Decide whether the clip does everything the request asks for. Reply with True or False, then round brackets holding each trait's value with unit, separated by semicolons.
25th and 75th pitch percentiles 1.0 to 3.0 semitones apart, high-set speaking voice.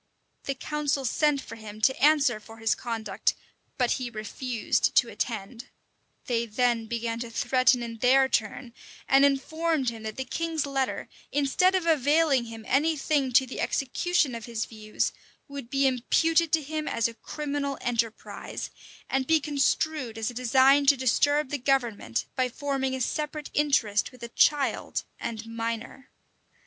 False (3.8 semitones; 260 Hz)